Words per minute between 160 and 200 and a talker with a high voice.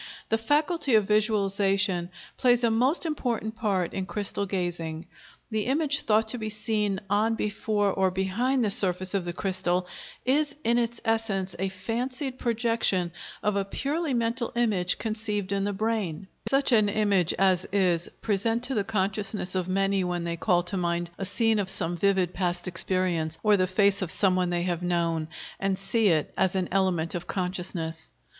Yes: average, 175 wpm; high, 195 Hz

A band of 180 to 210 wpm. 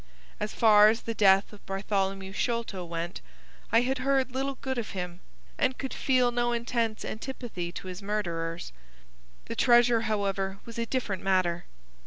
No: average, 160 wpm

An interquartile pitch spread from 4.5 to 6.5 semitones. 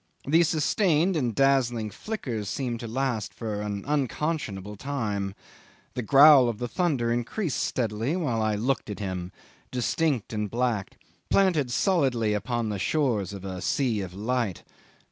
Yes: average, 5.2 semitones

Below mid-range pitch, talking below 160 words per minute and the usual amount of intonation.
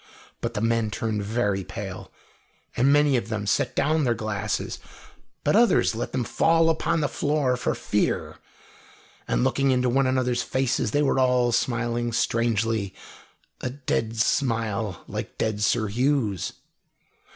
Yes: low, 120 Hz; average, 145 wpm; average, 3.2 semitones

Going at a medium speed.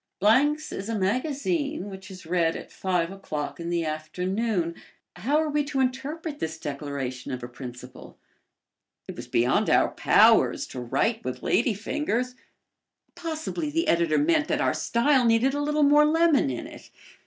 Yes: average, 160 wpm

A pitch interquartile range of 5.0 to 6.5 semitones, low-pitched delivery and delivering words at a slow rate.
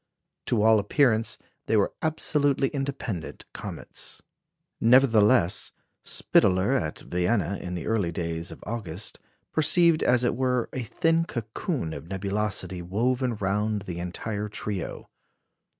Yes: average, 5.3 semitones; low, 110 Hz; slow, 120 wpm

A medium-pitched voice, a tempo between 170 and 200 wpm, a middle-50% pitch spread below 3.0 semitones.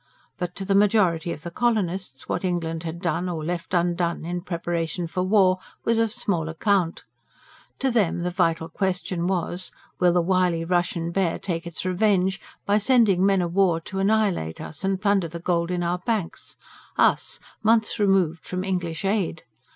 Yes: medium, 180 Hz; average, 175 wpm; narrow, 2.5 semitones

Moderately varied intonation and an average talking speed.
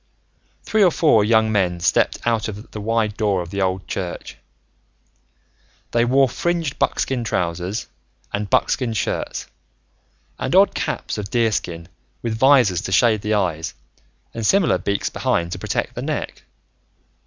Yes: average, 3.8 semitones; average, 145 wpm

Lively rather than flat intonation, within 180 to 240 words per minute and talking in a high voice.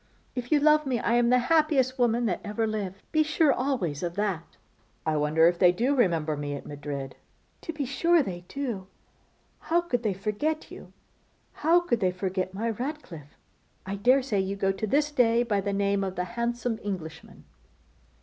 Yes: wide, 6.3 semitones; average, 185 wpm; high, 215 Hz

